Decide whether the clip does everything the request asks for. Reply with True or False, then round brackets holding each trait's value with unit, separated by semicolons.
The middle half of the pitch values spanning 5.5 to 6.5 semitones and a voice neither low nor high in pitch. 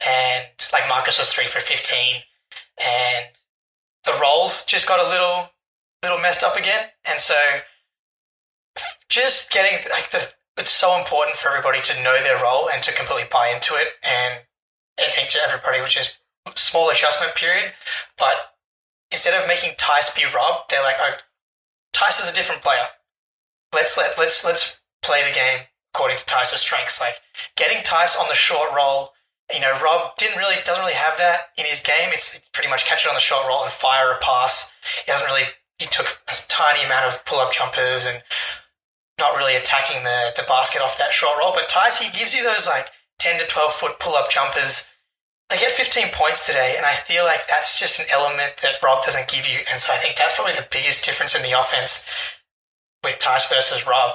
True (5.8 semitones; 150 Hz)